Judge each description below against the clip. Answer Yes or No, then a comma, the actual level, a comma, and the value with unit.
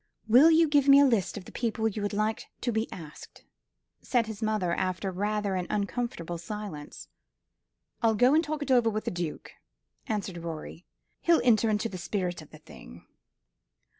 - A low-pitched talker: No, high, 215 Hz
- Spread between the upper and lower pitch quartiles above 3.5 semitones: Yes, average, 4.6 semitones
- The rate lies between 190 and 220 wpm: No, average, 180 wpm